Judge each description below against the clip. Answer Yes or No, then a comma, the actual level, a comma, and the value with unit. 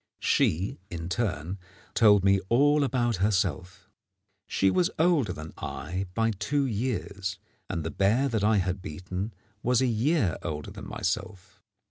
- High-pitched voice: No, low, 100 Hz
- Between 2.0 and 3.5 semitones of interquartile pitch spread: No, average, 4.7 semitones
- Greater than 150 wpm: No, average, 145 wpm